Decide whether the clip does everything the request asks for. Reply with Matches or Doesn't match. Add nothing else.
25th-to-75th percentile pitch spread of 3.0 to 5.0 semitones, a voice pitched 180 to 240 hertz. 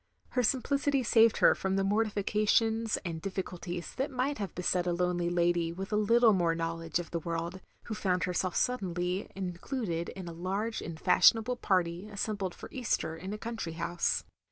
Matches